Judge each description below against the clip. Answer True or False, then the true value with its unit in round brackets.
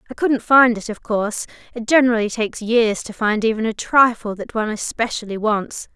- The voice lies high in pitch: True (225 Hz)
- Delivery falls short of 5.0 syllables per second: False (5.6 syllables/s)